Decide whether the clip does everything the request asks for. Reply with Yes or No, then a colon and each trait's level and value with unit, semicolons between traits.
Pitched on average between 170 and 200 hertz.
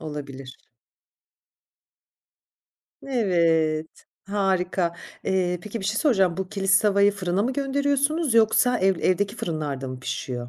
Yes: high, 190 Hz